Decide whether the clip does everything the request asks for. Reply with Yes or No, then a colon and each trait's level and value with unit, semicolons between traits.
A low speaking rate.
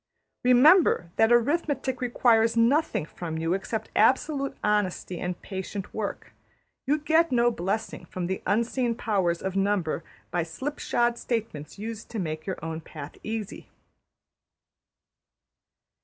Yes: slow, 125 wpm